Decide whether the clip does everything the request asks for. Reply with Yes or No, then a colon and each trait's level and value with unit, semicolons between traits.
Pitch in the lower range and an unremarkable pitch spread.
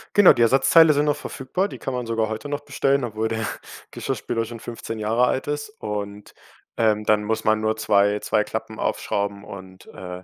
Yes: low, 110 Hz; average, 4.0 semitones